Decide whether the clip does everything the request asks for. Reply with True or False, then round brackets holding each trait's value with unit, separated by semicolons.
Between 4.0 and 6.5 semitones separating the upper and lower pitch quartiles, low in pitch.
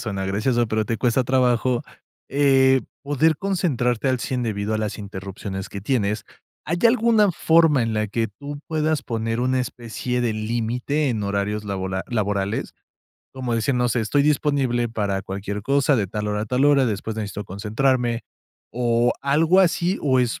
True (4.5 semitones; 120 Hz)